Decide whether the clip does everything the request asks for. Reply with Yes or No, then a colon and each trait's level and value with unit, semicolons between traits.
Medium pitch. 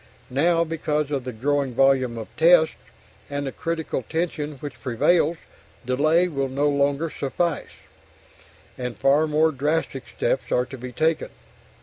Yes: medium, 145 Hz